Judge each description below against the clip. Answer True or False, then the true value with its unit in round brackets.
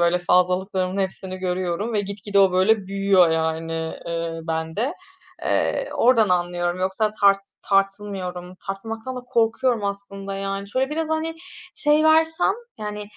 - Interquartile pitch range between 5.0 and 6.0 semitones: False (3.5 semitones)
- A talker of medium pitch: False (195 Hz)